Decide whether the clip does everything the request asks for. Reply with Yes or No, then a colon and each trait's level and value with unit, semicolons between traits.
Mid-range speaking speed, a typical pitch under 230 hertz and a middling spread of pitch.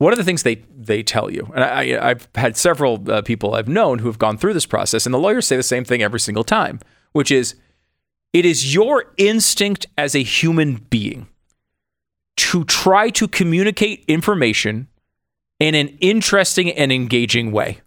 No: average, 180 wpm; medium, 140 Hz; wide, 8.5 semitones